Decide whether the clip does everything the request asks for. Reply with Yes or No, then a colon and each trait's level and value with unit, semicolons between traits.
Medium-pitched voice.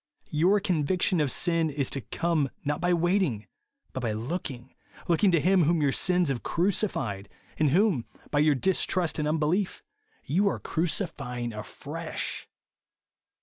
Yes: medium, 160 Hz